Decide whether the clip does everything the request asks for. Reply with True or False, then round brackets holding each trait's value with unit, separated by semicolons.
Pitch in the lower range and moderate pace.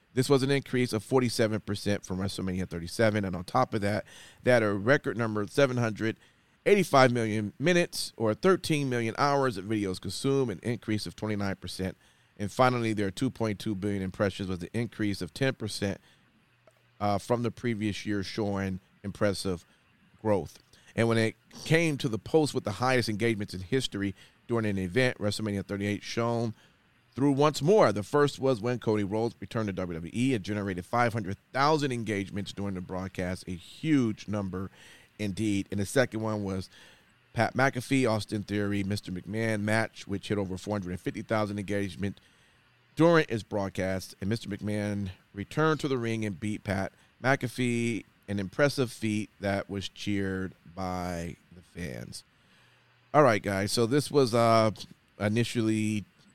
True (105 Hz; 160 wpm)